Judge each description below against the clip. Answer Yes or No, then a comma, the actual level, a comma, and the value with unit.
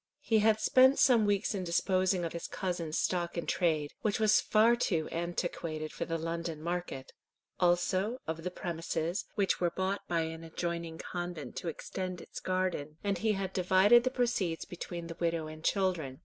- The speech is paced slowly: No, average, 175 wpm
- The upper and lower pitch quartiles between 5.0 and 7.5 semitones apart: No, average, 2.8 semitones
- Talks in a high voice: No, medium, 175 Hz